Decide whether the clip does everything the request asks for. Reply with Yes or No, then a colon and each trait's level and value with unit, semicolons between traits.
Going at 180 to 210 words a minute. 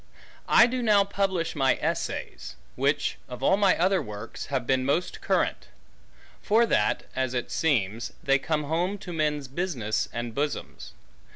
No: average, 155 wpm